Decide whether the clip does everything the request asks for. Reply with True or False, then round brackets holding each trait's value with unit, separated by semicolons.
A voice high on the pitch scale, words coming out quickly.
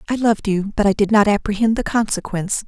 True (210 Hz; 225 wpm)